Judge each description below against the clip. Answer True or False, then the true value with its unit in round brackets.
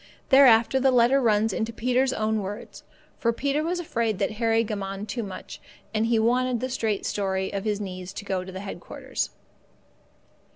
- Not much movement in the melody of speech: False (3.7 semitones)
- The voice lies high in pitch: True (225 Hz)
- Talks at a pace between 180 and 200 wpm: False (170 wpm)